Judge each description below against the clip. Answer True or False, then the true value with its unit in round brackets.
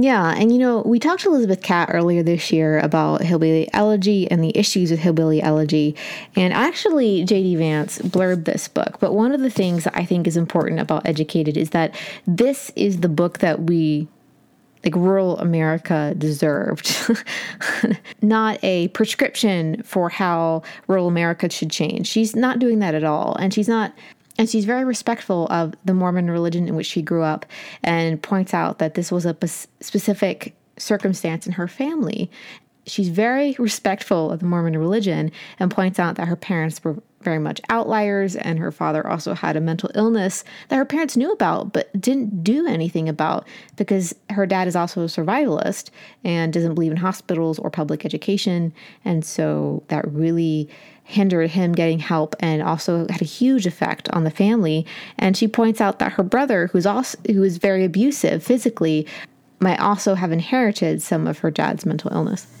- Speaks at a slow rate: False (180 wpm)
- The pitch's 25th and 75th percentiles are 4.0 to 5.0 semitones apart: True (4.4 semitones)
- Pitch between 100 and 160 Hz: False (185 Hz)